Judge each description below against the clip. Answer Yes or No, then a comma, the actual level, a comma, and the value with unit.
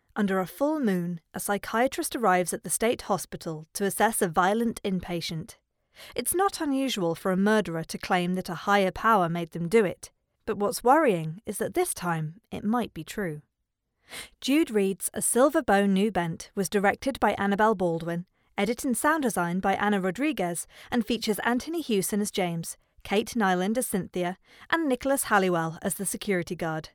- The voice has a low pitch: No, high, 200 Hz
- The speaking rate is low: No, average, 175 wpm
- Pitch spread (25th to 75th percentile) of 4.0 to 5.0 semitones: Yes, average, 4.5 semitones